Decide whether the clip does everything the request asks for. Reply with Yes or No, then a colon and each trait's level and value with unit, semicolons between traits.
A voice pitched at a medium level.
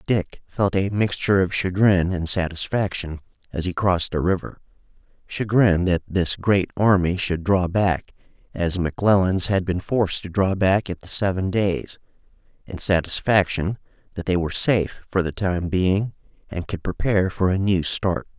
No: very low, 95 Hz